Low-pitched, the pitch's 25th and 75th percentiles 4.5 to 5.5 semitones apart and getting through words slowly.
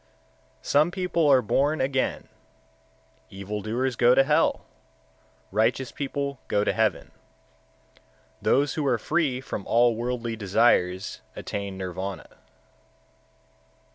Yes: low, 120 Hz; average, 5.0 semitones; slow, 110 wpm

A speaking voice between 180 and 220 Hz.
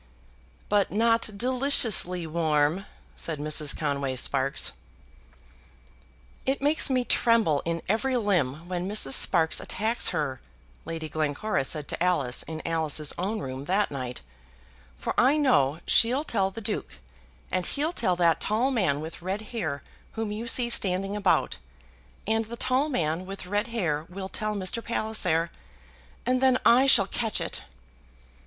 Yes: high, 190 Hz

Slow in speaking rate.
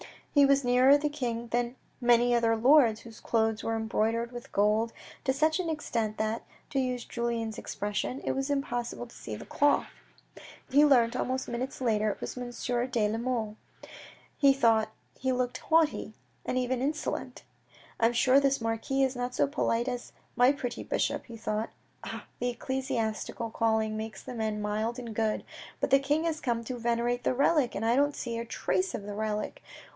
No: average, 190 wpm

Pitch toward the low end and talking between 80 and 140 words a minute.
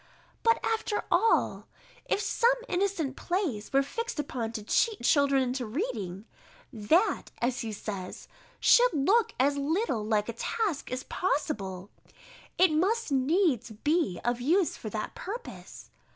No: very high, 280 Hz; slow, 135 wpm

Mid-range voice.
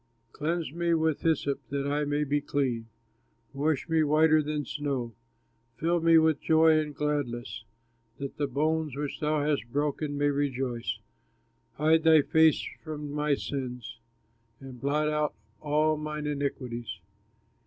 Yes: medium, 150 Hz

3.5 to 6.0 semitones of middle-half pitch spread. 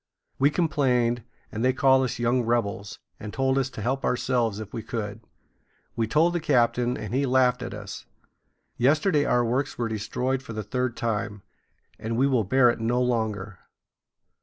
No: average, 2.9 semitones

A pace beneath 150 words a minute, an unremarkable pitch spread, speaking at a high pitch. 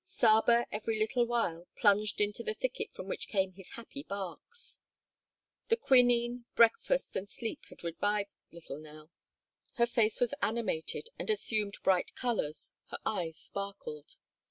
Yes: average, 140 wpm; average, 4.1 semitones; high, 215 Hz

